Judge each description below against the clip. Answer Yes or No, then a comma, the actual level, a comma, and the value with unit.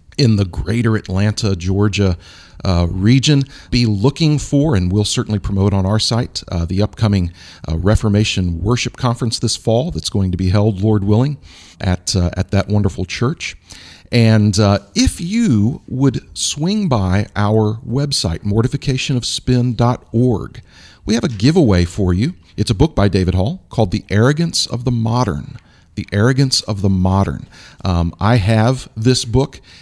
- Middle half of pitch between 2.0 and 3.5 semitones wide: No, average, 4.6 semitones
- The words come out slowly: No, average, 155 wpm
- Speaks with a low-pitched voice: Yes, low, 105 Hz